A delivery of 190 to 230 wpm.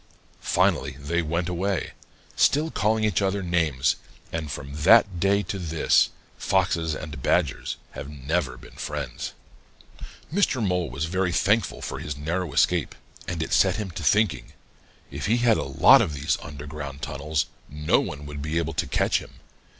No: average, 165 wpm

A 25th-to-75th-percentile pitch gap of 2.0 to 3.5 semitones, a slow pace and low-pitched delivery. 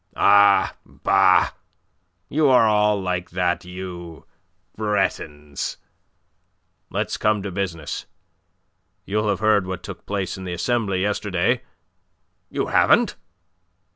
Yes: average, 2.8 semitones; slow, 105 wpm; low, 100 Hz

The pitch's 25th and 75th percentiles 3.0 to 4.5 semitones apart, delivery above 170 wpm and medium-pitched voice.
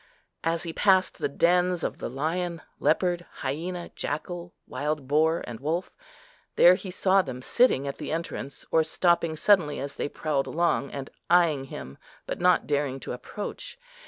No: average, 4.0 semitones; average, 160 wpm; medium, 165 Hz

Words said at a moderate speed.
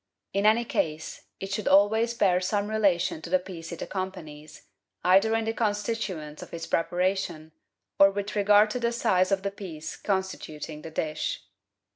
Yes: average, 165 wpm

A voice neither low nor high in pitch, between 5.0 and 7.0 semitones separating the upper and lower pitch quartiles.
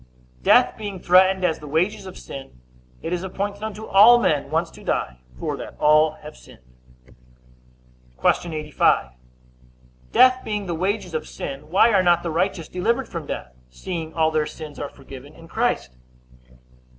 Yes: medium, 165 Hz; wide, 5.5 semitones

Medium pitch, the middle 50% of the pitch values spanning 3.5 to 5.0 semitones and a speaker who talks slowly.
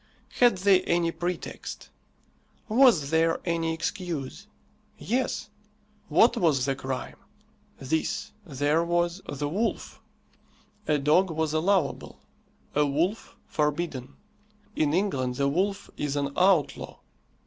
Yes: medium, 165 Hz; average, 4.4 semitones; slow, 110 wpm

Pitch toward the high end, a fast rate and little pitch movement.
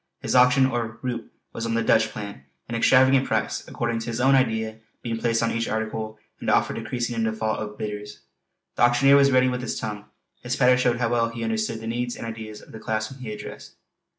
No: low, 115 Hz; fast, 230 wpm; narrow, 2.1 semitones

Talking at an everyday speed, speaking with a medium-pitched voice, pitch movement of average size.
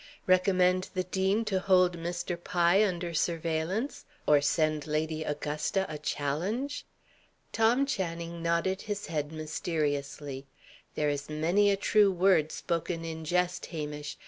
No: slow, 130 wpm; medium, 170 Hz; average, 3.5 semitones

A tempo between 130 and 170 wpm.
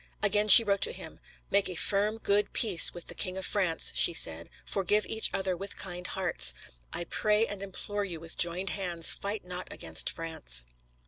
No: average, 190 wpm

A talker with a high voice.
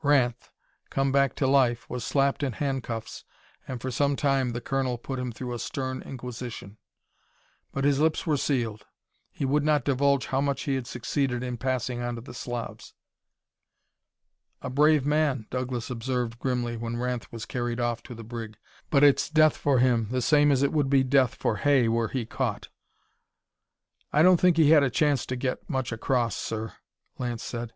No: low, 130 Hz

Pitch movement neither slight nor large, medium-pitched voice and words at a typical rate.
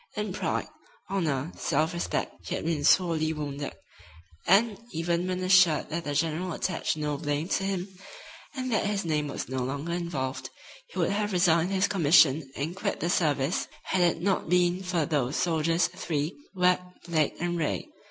Yes: average, 3.4 semitones; medium, 170 Hz; average, 170 wpm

